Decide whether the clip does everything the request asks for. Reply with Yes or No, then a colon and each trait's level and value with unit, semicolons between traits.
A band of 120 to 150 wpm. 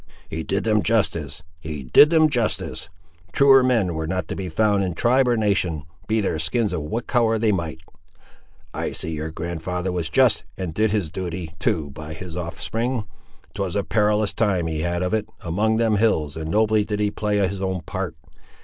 No: average, 195 wpm